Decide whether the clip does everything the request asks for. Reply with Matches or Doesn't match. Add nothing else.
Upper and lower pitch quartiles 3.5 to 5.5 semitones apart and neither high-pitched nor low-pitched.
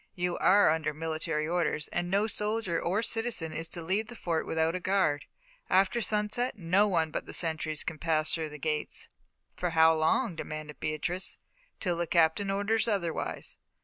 Matches